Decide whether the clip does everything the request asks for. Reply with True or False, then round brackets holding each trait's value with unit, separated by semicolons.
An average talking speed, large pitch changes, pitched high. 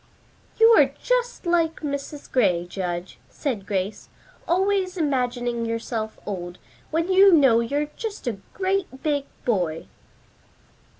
False (120 wpm; 8.2 semitones; 270 Hz)